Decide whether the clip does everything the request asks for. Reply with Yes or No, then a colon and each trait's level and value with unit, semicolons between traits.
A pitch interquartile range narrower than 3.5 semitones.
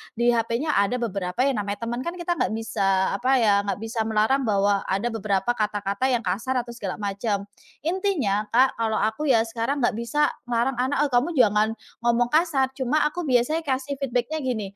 No: average, 4.0 semitones